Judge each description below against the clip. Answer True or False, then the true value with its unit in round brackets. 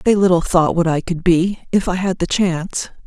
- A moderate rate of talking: False (235 wpm)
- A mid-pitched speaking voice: True (180 Hz)